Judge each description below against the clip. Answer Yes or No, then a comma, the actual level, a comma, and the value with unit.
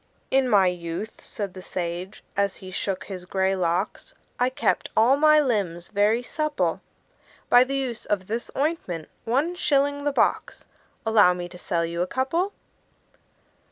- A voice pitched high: Yes, high, 210 Hz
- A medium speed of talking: Yes, average, 160 wpm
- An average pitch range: No, wide, 6.7 semitones